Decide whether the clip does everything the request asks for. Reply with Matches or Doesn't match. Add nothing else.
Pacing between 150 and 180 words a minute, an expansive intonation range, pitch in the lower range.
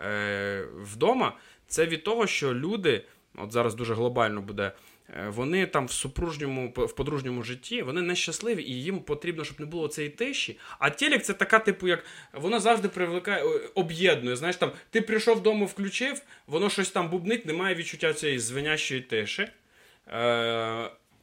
Doesn't match